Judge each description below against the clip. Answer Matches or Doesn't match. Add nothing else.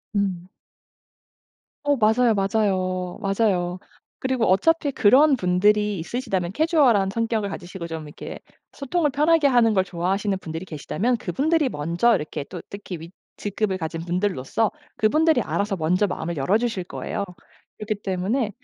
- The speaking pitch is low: Doesn't match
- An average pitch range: Matches